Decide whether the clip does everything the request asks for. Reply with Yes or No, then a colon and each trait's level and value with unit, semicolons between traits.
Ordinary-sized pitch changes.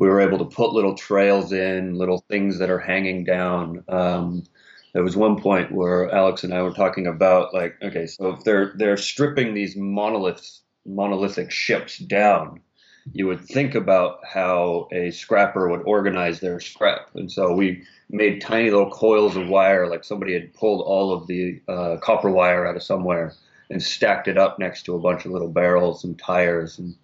No: narrow, 1.8 semitones